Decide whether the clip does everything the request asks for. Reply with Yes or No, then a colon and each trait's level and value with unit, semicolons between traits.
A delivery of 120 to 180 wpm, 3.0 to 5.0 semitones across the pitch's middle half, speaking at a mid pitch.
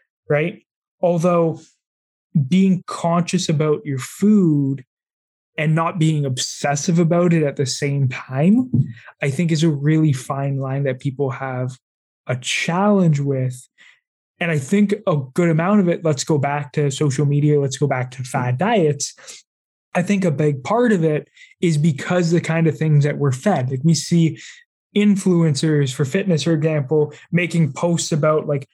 Yes: average, 165 wpm; average, 3.5 semitones; medium, 155 Hz